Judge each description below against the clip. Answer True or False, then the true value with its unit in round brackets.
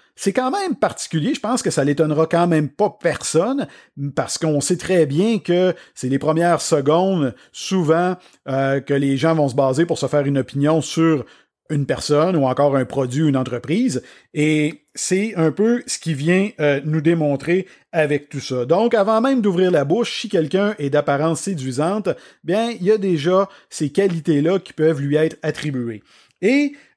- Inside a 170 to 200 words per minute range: True (180 wpm)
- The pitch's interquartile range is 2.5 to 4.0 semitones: False (4.5 semitones)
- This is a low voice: False (160 Hz)